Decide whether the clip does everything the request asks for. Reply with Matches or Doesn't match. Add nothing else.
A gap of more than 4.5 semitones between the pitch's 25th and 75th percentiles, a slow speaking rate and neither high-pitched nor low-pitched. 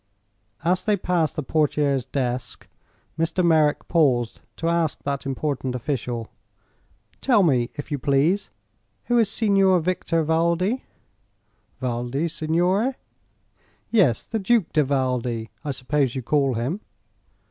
Matches